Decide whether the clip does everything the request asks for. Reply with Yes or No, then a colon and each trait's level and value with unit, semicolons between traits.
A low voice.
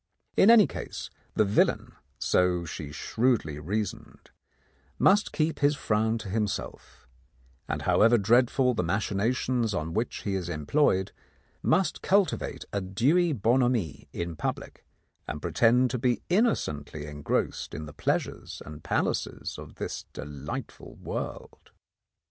Yes: low, 110 Hz